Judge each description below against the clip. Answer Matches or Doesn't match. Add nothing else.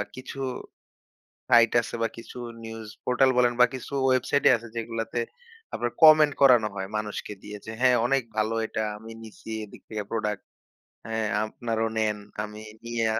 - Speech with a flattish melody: Matches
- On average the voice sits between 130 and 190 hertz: Doesn't match